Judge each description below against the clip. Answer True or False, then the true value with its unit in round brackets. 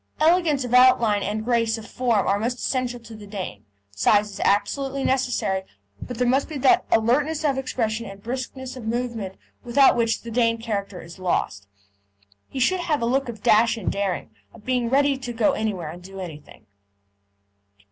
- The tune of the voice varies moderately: True (4.0 semitones)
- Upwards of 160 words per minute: True (180 wpm)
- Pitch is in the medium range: False (230 Hz)